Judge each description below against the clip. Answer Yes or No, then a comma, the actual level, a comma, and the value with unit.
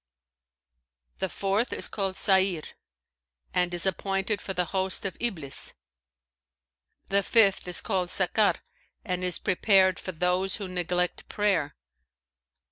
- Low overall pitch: No, high, 190 Hz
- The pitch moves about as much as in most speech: No, narrow, 1.7 semitones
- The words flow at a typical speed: No, slow, 125 wpm